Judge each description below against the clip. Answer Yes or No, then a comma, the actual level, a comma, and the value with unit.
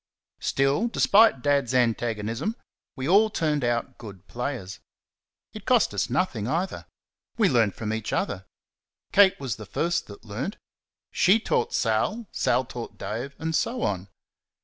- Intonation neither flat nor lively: No, wide, 8.7 semitones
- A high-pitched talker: No, low, 130 Hz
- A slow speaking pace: No, average, 145 wpm